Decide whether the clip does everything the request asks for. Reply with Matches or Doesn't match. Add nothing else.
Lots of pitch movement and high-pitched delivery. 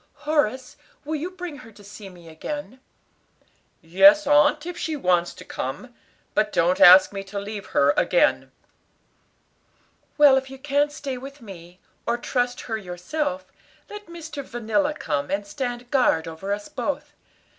Matches